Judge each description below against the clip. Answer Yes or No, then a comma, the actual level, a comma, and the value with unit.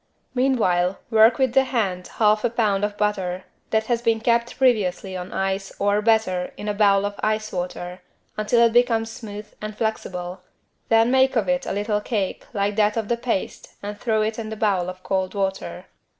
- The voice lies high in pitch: Yes, high, 210 Hz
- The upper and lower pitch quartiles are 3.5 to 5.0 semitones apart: No, average, 2.8 semitones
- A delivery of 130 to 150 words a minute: No, average, 190 wpm